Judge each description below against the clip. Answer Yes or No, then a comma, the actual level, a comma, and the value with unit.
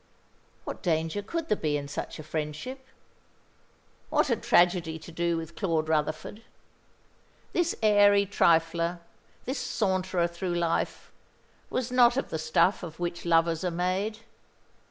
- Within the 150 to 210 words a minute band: No, slow, 135 wpm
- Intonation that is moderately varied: Yes, average, 3.9 semitones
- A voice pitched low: No, medium, 175 Hz